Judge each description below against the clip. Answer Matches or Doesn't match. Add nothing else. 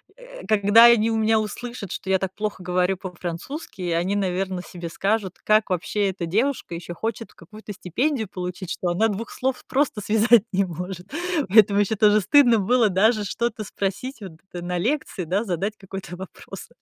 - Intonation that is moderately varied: Matches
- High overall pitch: Matches